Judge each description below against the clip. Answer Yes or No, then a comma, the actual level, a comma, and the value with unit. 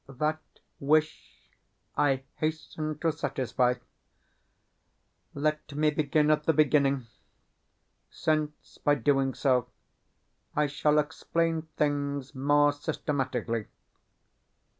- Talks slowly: Yes, slow, 90 wpm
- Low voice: No, medium, 145 Hz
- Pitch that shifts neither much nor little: No, narrow, 1.9 semitones